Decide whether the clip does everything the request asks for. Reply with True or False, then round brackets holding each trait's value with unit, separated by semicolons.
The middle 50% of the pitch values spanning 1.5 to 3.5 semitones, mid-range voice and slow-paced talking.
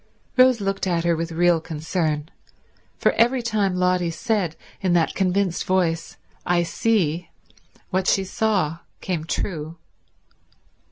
True (3.0 semitones; 180 Hz; 125 wpm)